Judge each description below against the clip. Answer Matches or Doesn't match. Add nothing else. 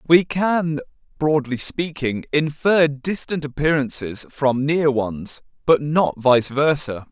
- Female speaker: Doesn't match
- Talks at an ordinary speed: Doesn't match